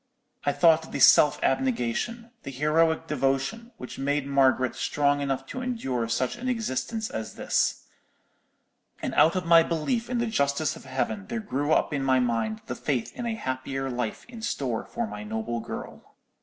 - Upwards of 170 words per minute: Yes, average, 180 wpm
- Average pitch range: No, wide, 8.5 semitones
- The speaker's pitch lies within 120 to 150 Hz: Yes, medium, 140 Hz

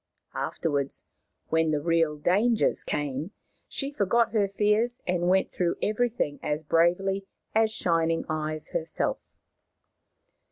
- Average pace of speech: No, slow, 115 wpm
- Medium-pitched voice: Yes, medium, 175 Hz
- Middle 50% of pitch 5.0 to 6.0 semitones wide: Yes, wide, 5.4 semitones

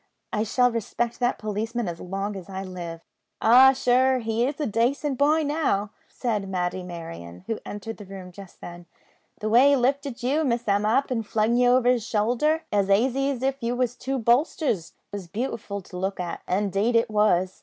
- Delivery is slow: No, average, 200 wpm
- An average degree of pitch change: Yes, average, 4.4 semitones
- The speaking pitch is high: Yes, high, 225 Hz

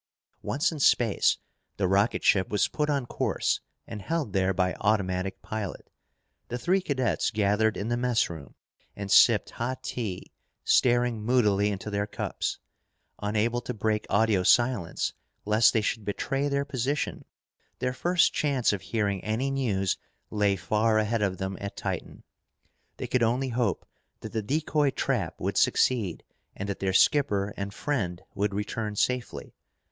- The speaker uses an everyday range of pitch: Yes, average, 4.0 semitones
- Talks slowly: No, average, 150 wpm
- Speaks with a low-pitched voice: Yes, low, 110 Hz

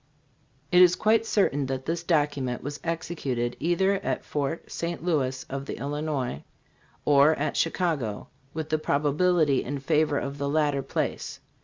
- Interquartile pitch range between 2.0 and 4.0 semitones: Yes, average, 3.3 semitones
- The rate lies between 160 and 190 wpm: No, average, 150 wpm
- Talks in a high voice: No, medium, 150 Hz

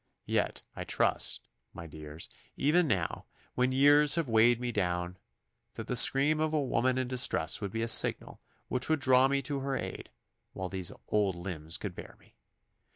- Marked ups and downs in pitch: Yes, wide, 6.7 semitones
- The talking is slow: No, average, 180 wpm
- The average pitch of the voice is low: Yes, low, 125 Hz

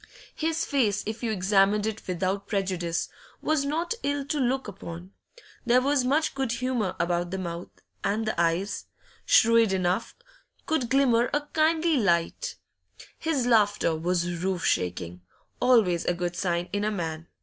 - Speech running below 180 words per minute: Yes, average, 150 wpm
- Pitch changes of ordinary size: No, wide, 6.7 semitones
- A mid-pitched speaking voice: No, high, 205 Hz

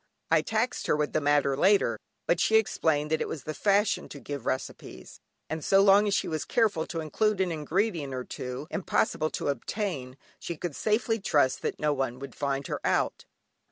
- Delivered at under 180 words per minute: No, average, 195 wpm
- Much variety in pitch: Yes, wide, 6.0 semitones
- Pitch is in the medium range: Yes, medium, 155 Hz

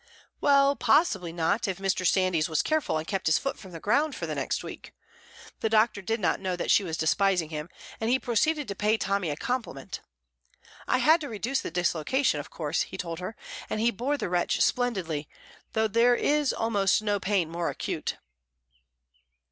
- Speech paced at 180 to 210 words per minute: Yes, average, 190 wpm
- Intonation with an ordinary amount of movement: No, wide, 5.7 semitones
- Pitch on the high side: Yes, high, 200 Hz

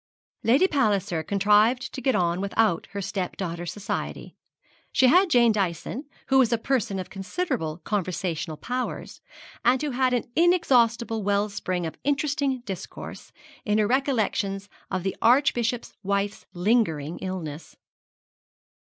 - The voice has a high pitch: Yes, high, 210 Hz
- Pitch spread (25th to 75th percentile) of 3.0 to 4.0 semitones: No, average, 5.3 semitones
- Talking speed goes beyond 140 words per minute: No, slow, 135 wpm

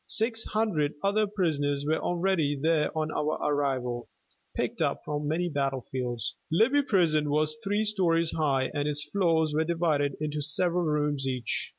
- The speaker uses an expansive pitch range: No, average, 3.5 semitones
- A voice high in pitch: No, medium, 155 Hz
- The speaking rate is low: No, average, 155 wpm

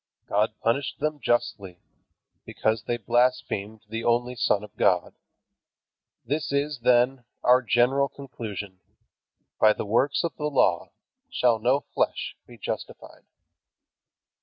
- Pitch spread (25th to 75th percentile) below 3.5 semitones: No, average, 3.8 semitones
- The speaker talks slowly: Yes, slow, 120 wpm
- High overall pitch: No, low, 120 Hz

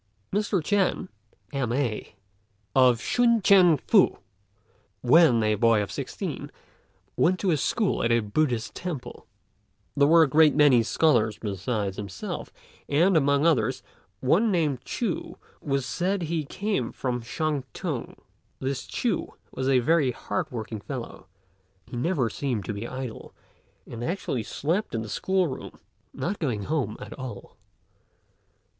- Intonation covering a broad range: Yes, wide, 6.3 semitones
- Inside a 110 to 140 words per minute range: Yes, slow, 135 wpm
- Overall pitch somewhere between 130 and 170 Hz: Yes, medium, 140 Hz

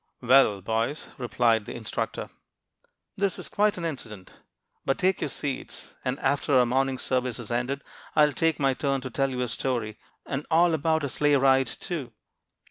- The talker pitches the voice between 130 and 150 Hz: Yes, low, 135 Hz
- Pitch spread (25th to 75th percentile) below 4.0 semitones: Yes, average, 3.3 semitones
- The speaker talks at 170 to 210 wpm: Yes, average, 180 wpm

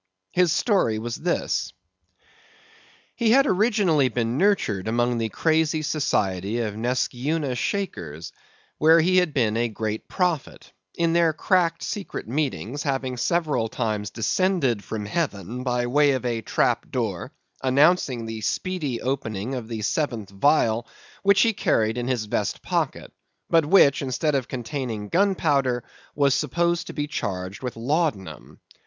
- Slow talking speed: No, average, 145 wpm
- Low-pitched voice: Yes, low, 130 Hz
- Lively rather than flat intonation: Yes, wide, 6.5 semitones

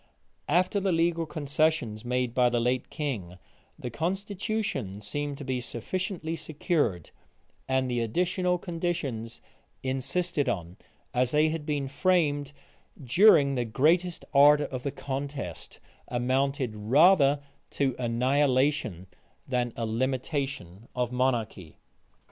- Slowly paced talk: Yes, slow, 115 wpm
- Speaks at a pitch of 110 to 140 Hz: Yes, low, 135 Hz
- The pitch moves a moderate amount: Yes, average, 4.5 semitones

